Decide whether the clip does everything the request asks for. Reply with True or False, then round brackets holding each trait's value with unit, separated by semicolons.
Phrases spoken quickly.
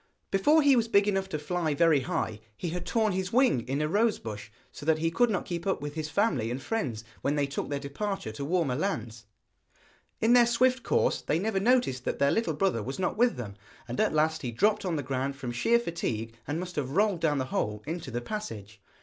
True (230 wpm)